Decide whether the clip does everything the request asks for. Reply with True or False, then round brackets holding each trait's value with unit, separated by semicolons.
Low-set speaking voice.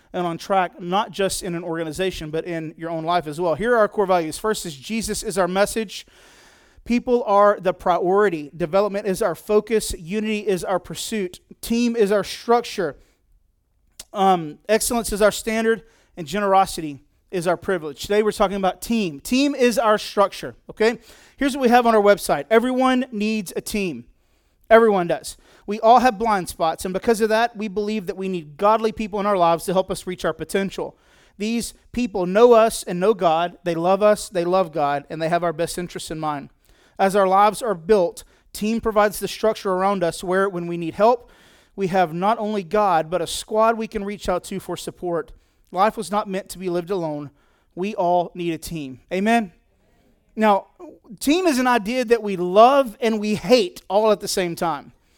False (200 Hz)